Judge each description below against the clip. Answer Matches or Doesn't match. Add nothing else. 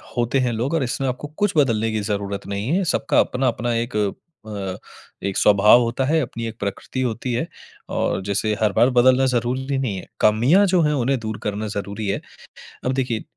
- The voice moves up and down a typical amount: Matches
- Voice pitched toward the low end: Matches